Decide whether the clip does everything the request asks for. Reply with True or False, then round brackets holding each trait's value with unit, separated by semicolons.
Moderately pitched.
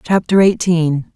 True (175 Hz)